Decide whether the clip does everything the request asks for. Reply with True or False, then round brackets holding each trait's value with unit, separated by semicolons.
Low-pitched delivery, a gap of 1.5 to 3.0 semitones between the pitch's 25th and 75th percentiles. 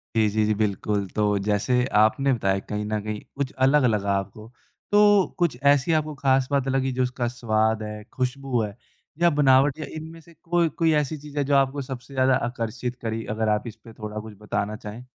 False (125 Hz; 4.4 semitones)